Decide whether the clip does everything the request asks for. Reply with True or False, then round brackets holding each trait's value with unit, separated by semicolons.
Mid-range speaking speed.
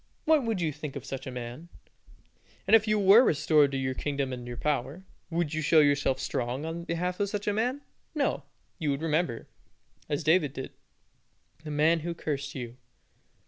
True (185 wpm)